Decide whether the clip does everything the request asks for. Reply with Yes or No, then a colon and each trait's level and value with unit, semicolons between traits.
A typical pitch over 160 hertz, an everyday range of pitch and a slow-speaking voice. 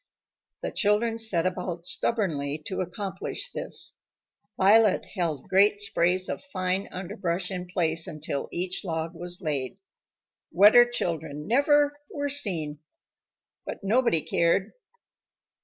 Yes: medium, 185 Hz; average, 4.0 semitones; slow, 115 wpm